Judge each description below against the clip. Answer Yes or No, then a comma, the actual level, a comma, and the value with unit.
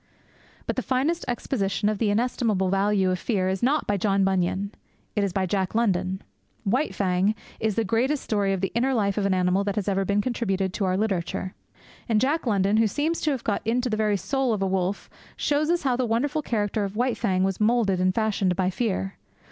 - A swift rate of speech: Yes, fast, 220 wpm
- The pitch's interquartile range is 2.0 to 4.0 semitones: Yes, average, 3.6 semitones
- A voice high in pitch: Yes, high, 205 Hz